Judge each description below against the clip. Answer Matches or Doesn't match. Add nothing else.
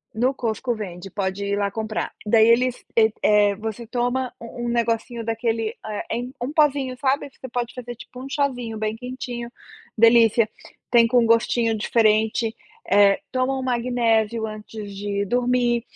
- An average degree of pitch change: Doesn't match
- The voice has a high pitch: Matches